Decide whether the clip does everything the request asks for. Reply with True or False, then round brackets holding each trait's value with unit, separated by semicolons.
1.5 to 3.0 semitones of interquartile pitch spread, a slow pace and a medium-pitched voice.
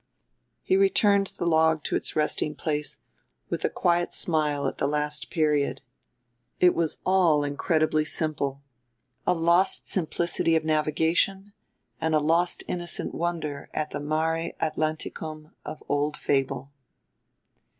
True (2.4 semitones; 130 wpm; 155 Hz)